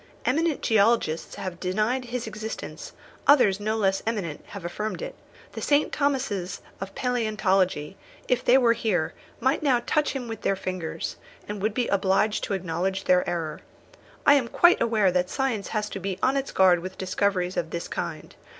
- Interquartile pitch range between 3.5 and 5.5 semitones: Yes, average, 4.8 semitones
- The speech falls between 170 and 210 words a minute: Yes, average, 175 wpm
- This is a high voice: Yes, high, 210 Hz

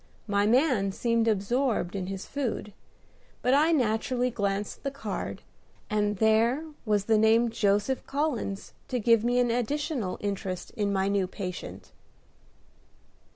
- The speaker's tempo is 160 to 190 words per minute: No, average, 140 wpm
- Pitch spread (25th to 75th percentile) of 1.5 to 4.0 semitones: Yes, average, 3.7 semitones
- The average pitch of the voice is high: Yes, high, 220 Hz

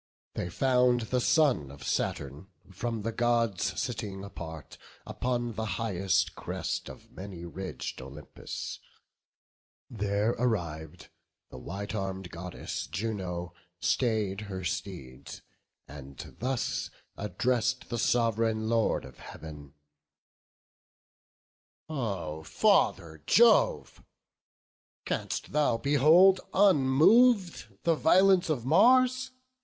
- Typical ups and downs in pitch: No, wide, 6.3 semitones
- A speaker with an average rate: No, slow, 95 wpm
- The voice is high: No, low, 110 Hz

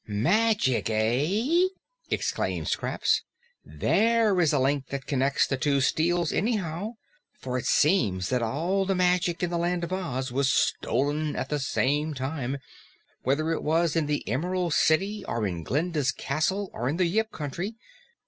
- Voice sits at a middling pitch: Yes, medium, 155 Hz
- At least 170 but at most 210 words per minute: No, average, 160 wpm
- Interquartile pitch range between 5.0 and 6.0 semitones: Yes, wide, 5.4 semitones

